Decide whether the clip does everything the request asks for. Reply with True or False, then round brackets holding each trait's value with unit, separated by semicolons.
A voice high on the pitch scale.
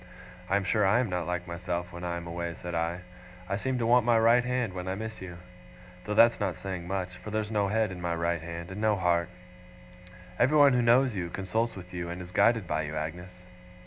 False (95 Hz)